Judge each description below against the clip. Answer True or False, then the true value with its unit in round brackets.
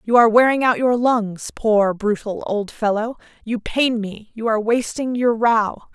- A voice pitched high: True (225 Hz)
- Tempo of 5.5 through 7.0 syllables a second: False (4.4 syllables/s)